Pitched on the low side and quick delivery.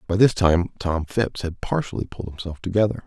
No: very low, 95 Hz; average, 195 wpm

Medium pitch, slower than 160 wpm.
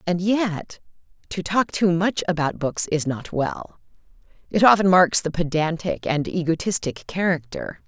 Yes: medium, 170 Hz; average, 145 wpm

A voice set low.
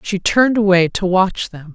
No: high, 190 Hz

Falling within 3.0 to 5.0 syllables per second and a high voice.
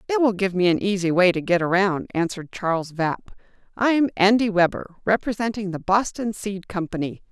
No: 5.3 syllables/s; high, 195 Hz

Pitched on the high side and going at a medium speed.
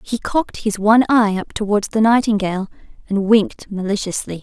Yes: high, 210 Hz; average, 165 wpm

